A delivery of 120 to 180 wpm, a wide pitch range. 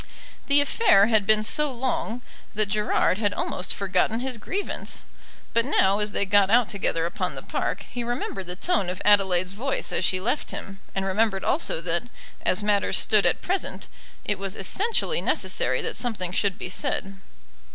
No: average, 175 wpm; average, 4.0 semitones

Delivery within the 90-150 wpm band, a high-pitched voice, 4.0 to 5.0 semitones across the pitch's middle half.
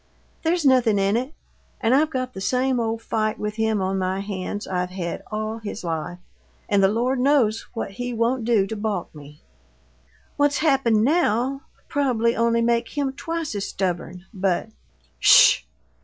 No: average, 170 wpm; high, 225 Hz; average, 4.6 semitones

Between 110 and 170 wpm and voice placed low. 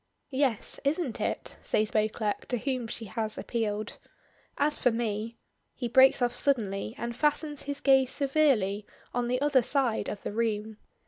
No: average, 160 wpm; high, 240 Hz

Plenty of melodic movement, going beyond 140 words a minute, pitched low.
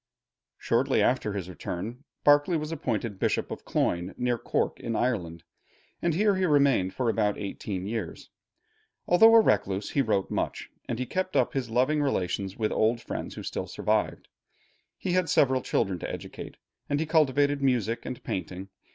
Yes: wide, 6.4 semitones; average, 170 wpm; low, 120 Hz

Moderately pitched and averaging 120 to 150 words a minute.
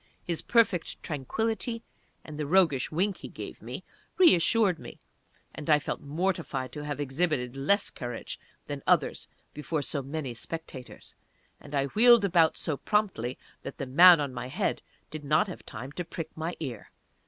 No: medium, 155 Hz; average, 165 wpm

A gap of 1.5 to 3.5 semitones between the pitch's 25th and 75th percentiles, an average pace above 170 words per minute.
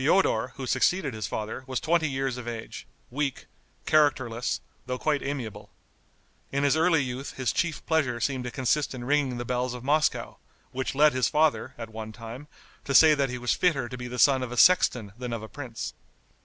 Yes: average, 3.2 semitones; average, 200 wpm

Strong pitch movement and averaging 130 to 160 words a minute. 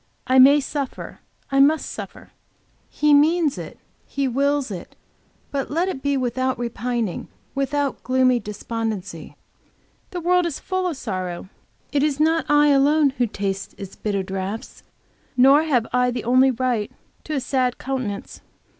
No: average, 4.0 semitones; average, 150 wpm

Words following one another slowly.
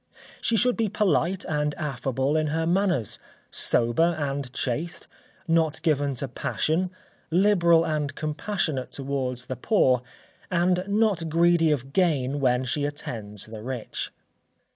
Yes: slow, 130 wpm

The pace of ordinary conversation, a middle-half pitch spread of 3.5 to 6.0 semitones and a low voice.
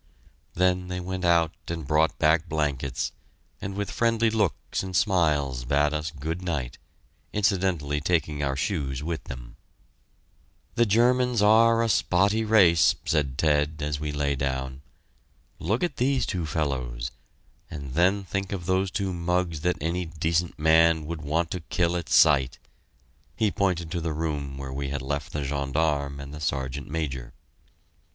Yes: average, 155 wpm; average, 4.3 semitones; very low, 80 Hz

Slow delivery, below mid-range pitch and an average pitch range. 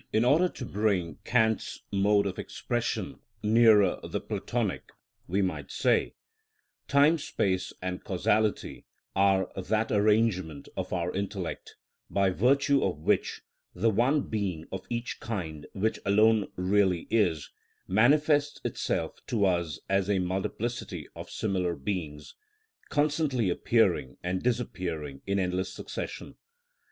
Yes: slow, 125 wpm; low, 100 Hz; average, 3.9 semitones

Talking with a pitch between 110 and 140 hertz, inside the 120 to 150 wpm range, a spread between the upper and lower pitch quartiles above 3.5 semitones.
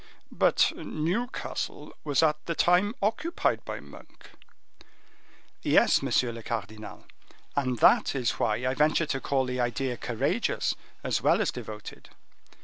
Yes: low, 135 Hz; slow, 135 wpm; average, 5.3 semitones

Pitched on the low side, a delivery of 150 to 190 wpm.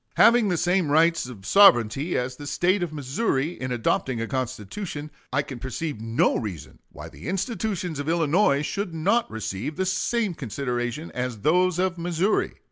No: medium, 155 Hz; average, 165 wpm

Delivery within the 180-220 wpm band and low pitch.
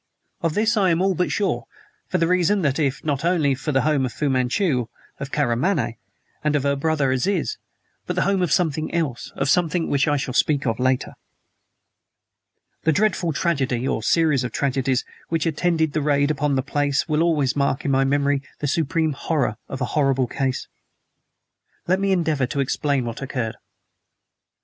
No: average, 185 wpm; medium, 145 Hz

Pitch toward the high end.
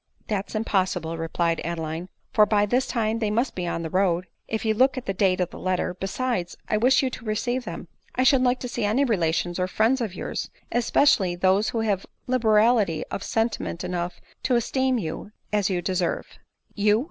Yes: high, 210 Hz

